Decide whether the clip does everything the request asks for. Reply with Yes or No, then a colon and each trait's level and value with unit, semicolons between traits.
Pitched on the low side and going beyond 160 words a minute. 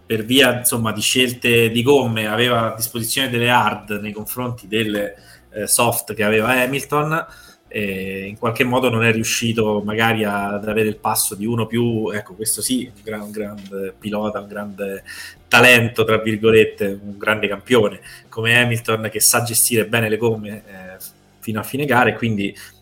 Yes: low, 110 Hz; fast, 170 wpm